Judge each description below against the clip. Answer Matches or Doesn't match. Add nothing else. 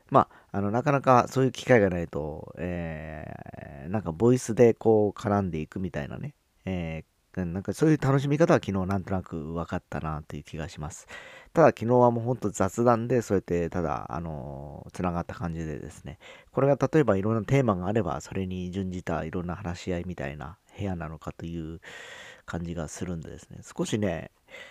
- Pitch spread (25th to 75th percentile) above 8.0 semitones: Doesn't match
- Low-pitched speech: Matches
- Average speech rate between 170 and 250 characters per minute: Doesn't match